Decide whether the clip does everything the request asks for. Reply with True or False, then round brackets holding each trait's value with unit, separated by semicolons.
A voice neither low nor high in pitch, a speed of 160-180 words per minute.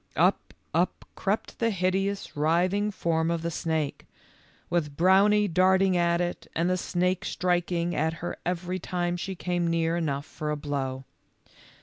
False (175 Hz; 150 wpm)